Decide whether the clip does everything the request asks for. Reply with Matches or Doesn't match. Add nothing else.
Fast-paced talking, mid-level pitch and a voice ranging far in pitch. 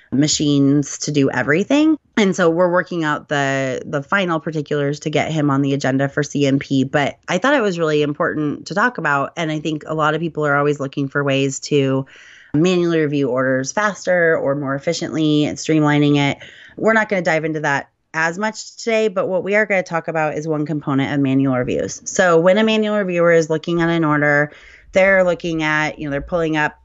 Doesn't match